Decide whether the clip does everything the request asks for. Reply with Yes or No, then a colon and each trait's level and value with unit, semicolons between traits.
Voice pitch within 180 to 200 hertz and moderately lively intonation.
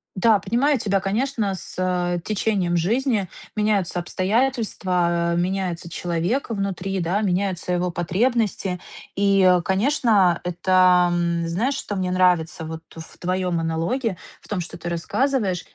Yes: medium, 185 Hz; average, 3.2 semitones